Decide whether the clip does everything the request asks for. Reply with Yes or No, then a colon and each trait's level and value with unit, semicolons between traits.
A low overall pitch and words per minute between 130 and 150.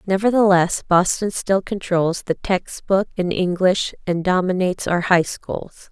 No: medium, 185 Hz; average, 140 wpm